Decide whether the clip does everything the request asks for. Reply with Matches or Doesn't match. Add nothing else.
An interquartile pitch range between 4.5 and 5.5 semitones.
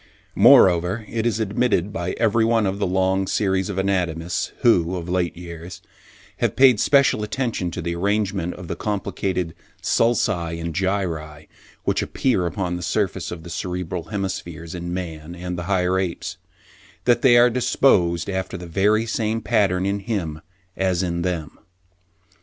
Doesn't match